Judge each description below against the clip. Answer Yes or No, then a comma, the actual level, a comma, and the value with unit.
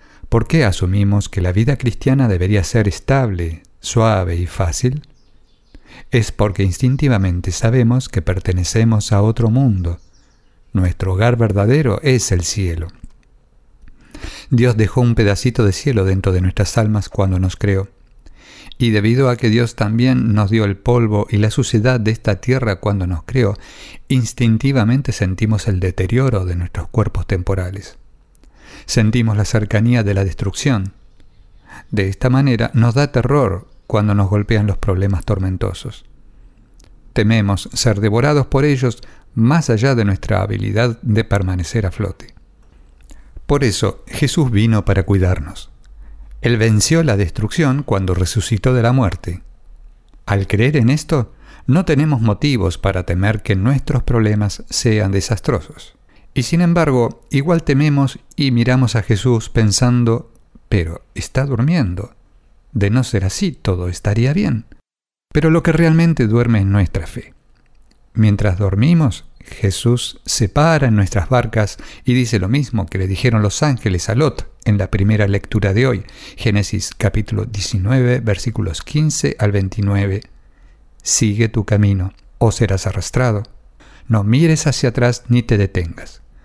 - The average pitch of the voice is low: Yes, low, 110 Hz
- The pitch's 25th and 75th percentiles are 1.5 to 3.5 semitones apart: No, average, 4.1 semitones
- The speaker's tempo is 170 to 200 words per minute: No, average, 140 wpm